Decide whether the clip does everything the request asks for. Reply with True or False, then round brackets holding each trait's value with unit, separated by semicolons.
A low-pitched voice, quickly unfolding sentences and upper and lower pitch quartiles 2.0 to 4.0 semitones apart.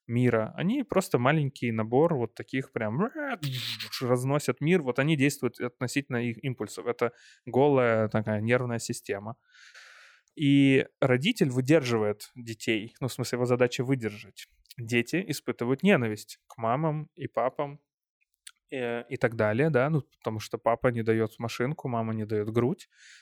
False (125 Hz; 140 wpm; 3.6 semitones)